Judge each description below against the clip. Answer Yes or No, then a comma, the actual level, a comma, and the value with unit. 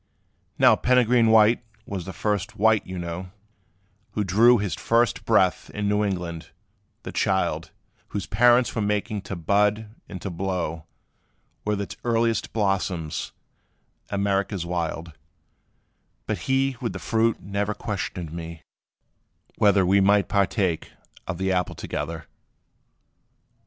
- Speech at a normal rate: No, slow, 125 wpm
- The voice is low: Yes, low, 100 Hz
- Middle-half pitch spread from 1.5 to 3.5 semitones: Yes, average, 3.2 semitones